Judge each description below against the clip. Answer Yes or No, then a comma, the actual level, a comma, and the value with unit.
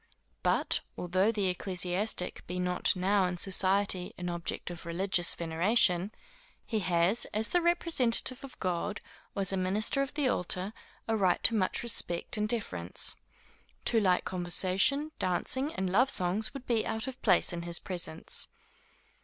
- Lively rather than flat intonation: No, average, 3.9 semitones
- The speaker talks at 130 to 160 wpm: Yes, average, 155 wpm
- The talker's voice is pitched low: No, high, 190 Hz